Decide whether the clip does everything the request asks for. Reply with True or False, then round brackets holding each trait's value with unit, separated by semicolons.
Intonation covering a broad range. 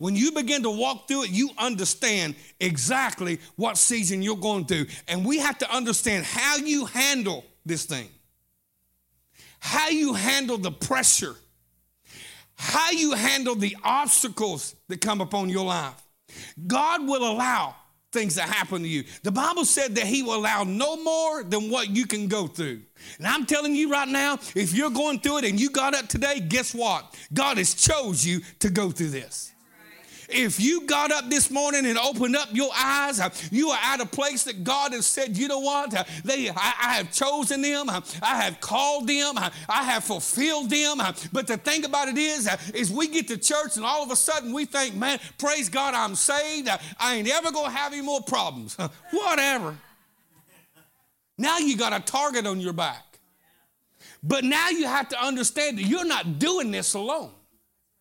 True (7.0 semitones)